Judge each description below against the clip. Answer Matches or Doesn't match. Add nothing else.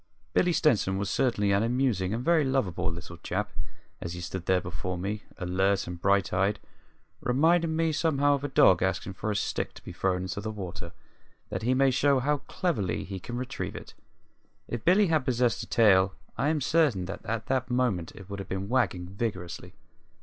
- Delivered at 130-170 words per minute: Doesn't match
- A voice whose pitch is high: Doesn't match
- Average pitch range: Doesn't match